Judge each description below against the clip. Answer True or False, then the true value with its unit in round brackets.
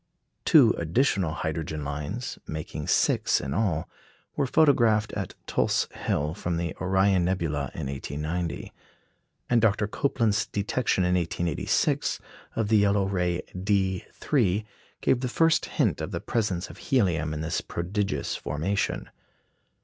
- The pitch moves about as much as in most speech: True (4.7 semitones)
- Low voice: True (95 Hz)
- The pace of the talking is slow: True (130 wpm)